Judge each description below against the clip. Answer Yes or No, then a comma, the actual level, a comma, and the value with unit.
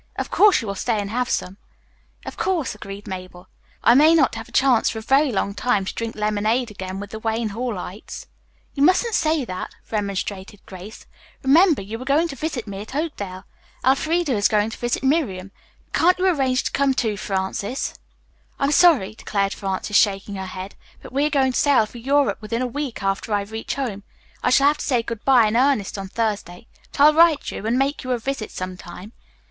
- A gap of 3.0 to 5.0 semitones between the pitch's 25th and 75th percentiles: No, wide, 5.5 semitones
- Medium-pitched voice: No, high, 230 Hz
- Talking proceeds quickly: Yes, fast, 210 wpm